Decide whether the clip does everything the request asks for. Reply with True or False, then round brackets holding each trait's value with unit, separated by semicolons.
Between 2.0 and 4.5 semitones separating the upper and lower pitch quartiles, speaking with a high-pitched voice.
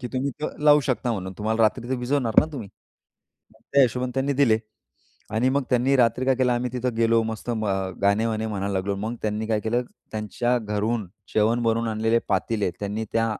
False (2.5 semitones; 115 Hz)